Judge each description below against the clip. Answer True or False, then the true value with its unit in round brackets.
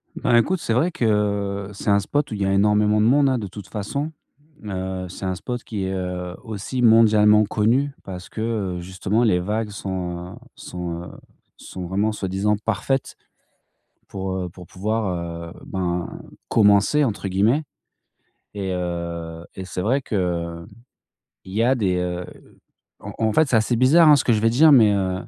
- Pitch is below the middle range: True (100 Hz)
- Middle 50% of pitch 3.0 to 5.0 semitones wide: True (3.5 semitones)